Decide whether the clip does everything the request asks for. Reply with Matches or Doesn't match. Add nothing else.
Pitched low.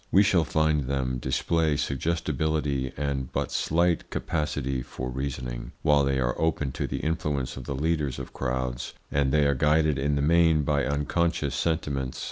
Matches